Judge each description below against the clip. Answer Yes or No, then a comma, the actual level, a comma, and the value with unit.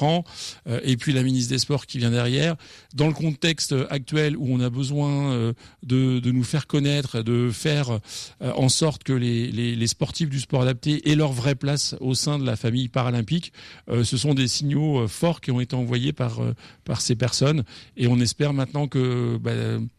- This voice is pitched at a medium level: No, low, 130 Hz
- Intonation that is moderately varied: Yes, average, 3.1 semitones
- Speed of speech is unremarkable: Yes, average, 190 wpm